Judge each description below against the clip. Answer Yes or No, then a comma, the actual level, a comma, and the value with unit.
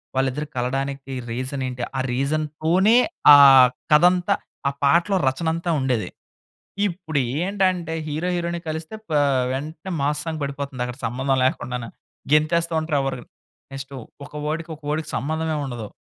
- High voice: No, medium, 150 Hz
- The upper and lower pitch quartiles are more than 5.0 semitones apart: No, average, 3.7 semitones